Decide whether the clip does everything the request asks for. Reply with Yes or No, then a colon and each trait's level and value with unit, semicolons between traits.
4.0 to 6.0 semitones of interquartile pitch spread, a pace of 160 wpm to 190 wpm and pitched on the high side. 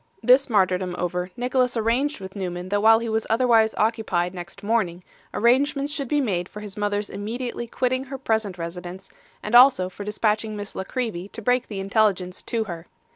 Yes: average, 4.4 semitones; average, 180 wpm; high, 215 Hz